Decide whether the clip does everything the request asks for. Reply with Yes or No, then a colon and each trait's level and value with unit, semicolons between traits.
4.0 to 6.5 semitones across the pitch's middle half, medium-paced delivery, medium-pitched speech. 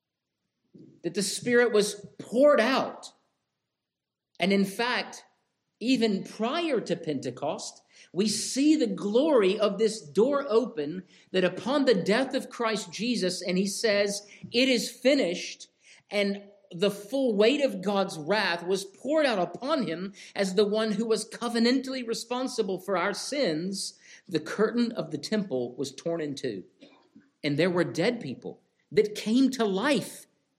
No: average, 4.6 semitones; average, 145 wpm; high, 210 Hz